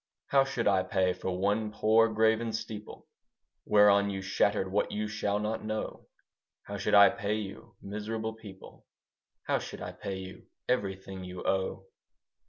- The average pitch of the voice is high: No, low, 105 Hz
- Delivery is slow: No, average, 155 wpm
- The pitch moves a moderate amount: No, narrow, 2.2 semitones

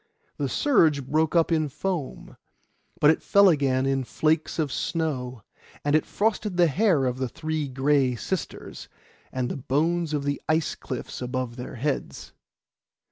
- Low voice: No, medium, 145 Hz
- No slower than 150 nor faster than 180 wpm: Yes, average, 155 wpm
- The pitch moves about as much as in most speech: Yes, average, 3.7 semitones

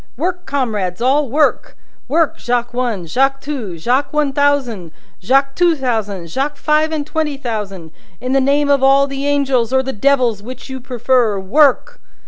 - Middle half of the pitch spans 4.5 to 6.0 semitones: No, average, 3.6 semitones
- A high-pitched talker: Yes, very high, 265 Hz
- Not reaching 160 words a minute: No, average, 165 wpm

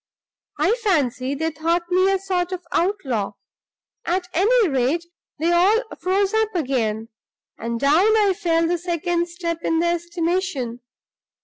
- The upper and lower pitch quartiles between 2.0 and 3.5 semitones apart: No, average, 4.0 semitones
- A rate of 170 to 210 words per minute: No, average, 140 wpm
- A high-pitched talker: Yes, very high, 345 Hz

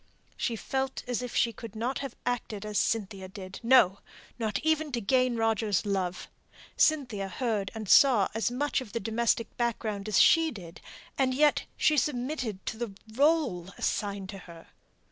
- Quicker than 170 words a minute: No, average, 165 wpm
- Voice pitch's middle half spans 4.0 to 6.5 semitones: Yes, average, 4.4 semitones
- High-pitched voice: Yes, high, 225 Hz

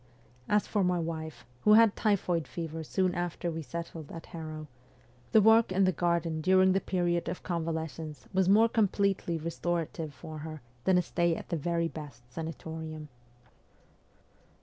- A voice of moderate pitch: Yes, medium, 170 Hz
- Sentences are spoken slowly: No, average, 155 wpm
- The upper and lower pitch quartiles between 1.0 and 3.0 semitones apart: Yes, average, 2.7 semitones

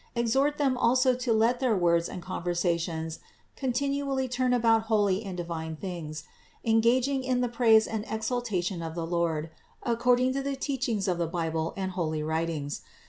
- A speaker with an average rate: Yes, average, 160 wpm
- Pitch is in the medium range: No, high, 220 Hz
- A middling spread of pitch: No, wide, 6.6 semitones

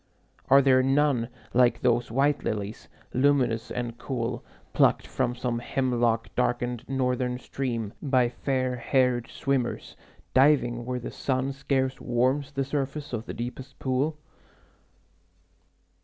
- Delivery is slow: Yes, slow, 125 wpm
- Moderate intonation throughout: No, narrow, 2.1 semitones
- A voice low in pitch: Yes, low, 125 Hz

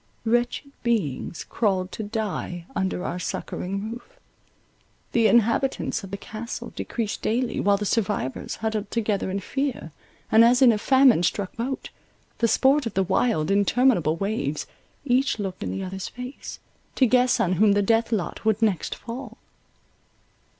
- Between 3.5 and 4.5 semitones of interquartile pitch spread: Yes, average, 3.8 semitones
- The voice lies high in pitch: Yes, high, 220 Hz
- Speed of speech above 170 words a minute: No, average, 155 wpm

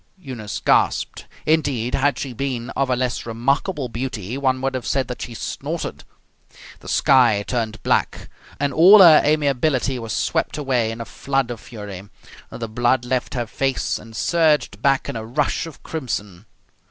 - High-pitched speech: No, low, 130 Hz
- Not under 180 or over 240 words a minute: No, average, 165 wpm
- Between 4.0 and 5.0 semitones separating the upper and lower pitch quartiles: No, average, 3.3 semitones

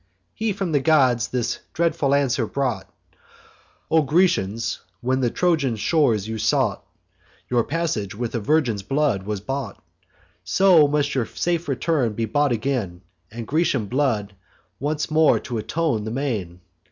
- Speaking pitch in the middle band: No, low, 130 Hz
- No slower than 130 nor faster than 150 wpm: Yes, average, 140 wpm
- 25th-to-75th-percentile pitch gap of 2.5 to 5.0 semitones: No, wide, 5.4 semitones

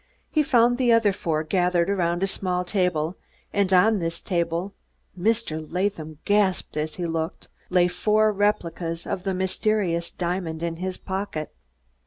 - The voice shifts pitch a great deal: No, average, 3.2 semitones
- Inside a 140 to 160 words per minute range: Yes, average, 150 wpm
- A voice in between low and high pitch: Yes, medium, 180 Hz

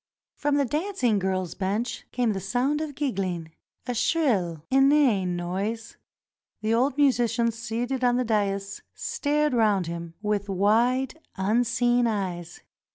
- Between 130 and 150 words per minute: Yes, slow, 135 wpm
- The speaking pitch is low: No, high, 230 Hz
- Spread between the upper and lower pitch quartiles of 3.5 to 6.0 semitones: Yes, average, 4.7 semitones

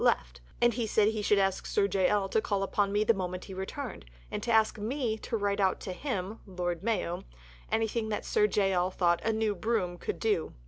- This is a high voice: Yes, high, 205 Hz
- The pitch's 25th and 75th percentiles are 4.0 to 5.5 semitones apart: No, average, 2.9 semitones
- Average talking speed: No, fast, 225 wpm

